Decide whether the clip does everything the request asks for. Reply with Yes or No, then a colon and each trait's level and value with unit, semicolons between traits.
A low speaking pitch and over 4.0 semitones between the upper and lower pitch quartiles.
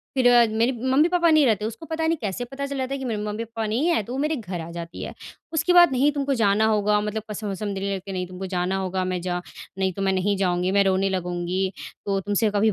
No: high, 210 Hz; wide, 5.4 semitones